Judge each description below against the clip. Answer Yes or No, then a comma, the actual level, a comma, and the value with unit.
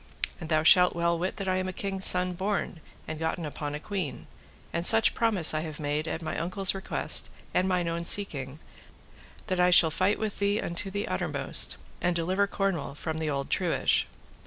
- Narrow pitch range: No, average, 3.3 semitones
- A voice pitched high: No, medium, 175 Hz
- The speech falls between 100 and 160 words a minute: No, average, 195 wpm